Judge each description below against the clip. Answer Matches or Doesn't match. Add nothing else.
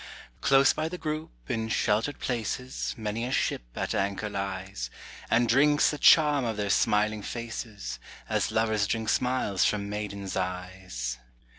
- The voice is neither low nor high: Doesn't match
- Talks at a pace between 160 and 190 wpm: Doesn't match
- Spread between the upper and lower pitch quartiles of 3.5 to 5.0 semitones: Matches